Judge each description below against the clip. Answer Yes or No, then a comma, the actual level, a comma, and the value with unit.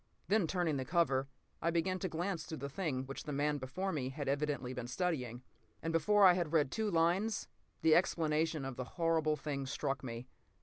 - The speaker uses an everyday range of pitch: Yes, average, 4.1 semitones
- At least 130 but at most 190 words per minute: No, fast, 205 wpm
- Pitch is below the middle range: No, medium, 155 Hz